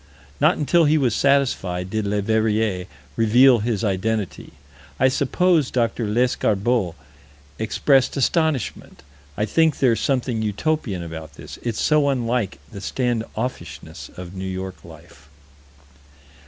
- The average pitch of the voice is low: Yes, low, 110 Hz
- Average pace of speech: No, slow, 120 wpm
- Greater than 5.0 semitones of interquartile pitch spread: Yes, wide, 5.5 semitones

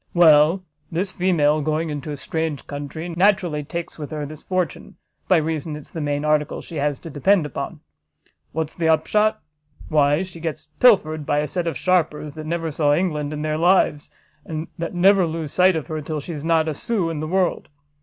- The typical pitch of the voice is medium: Yes, medium, 160 Hz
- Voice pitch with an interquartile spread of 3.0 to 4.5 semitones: No, narrow, 2.5 semitones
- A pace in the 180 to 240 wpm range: Yes, average, 200 wpm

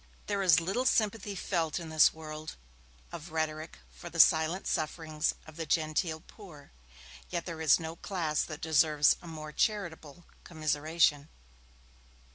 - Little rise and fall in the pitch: Yes, narrow, 2.1 semitones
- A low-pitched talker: No, medium, 160 Hz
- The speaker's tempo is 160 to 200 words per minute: No, average, 140 wpm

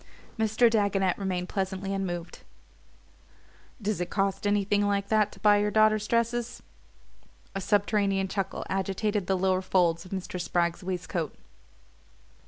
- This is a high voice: Yes, high, 195 Hz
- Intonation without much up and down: Yes, narrow, 1.9 semitones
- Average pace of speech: No, slow, 130 wpm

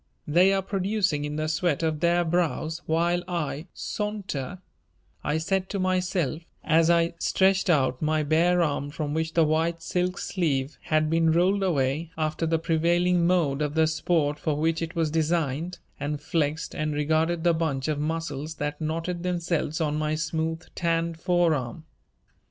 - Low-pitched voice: No, medium, 160 Hz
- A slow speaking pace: No, average, 165 wpm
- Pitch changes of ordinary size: No, narrow, 2.2 semitones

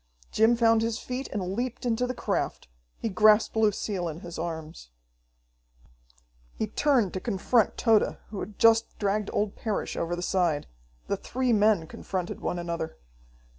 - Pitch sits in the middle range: No, high, 210 Hz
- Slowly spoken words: No, average, 155 wpm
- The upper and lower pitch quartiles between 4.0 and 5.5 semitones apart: Yes, average, 4.3 semitones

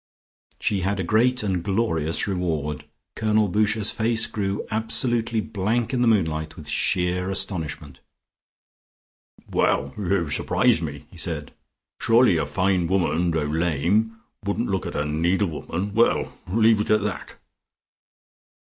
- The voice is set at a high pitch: No, very low, 95 Hz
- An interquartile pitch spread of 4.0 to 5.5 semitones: Yes, average, 4.8 semitones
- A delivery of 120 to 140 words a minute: Yes, slow, 135 wpm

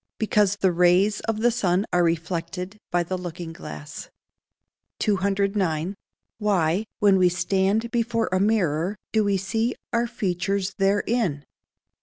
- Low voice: No, high, 195 Hz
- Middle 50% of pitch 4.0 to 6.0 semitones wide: No, average, 3.0 semitones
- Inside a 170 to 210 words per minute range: No, slow, 135 wpm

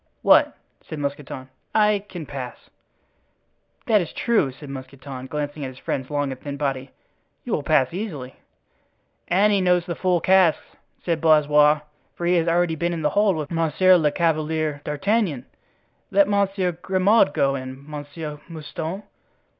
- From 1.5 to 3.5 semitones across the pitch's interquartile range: No, average, 4.1 semitones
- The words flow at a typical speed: Yes, average, 155 wpm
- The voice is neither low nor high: Yes, medium, 155 Hz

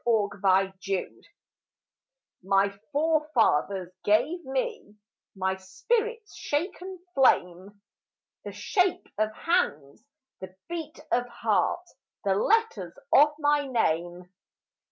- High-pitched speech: Yes, high, 225 Hz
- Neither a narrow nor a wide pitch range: No, wide, 8.8 semitones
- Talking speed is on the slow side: Yes, slow, 90 wpm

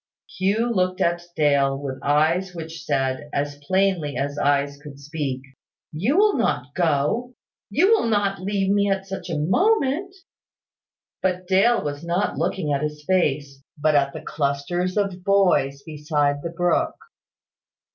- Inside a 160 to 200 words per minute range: No, average, 145 wpm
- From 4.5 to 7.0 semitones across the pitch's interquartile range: Yes, average, 5.3 semitones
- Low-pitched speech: No, medium, 165 Hz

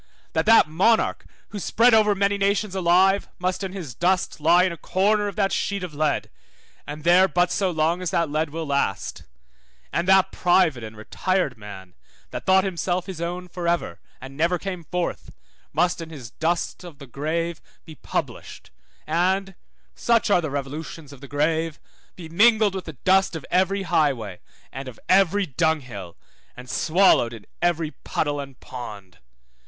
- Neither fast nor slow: Yes, average, 170 wpm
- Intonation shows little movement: No, average, 4.6 semitones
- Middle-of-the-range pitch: Yes, medium, 170 Hz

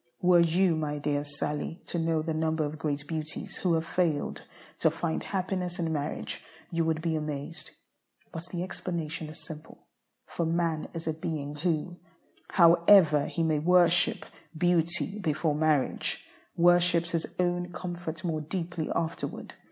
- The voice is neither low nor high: Yes, medium, 165 Hz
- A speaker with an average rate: Yes, average, 150 wpm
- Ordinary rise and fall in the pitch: No, narrow, 2.1 semitones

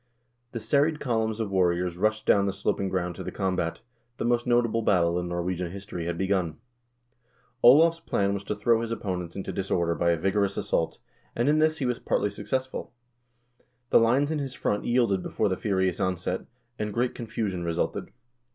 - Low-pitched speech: Yes, low, 100 Hz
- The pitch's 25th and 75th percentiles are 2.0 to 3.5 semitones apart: No, average, 4.6 semitones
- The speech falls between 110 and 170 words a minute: No, average, 190 wpm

